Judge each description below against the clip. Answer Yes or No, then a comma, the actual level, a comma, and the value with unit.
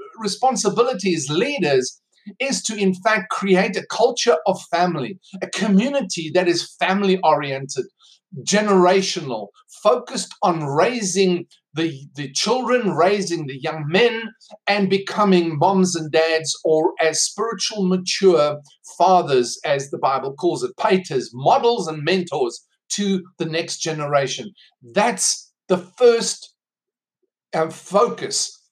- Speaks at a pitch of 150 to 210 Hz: Yes, medium, 185 Hz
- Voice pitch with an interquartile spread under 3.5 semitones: No, average, 5.1 semitones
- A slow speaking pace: Yes, slow, 115 wpm